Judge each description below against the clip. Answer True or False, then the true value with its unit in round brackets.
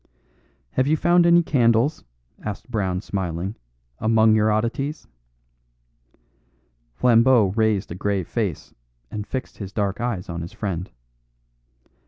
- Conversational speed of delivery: False (120 wpm)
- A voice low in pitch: True (110 Hz)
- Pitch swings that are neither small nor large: True (4.2 semitones)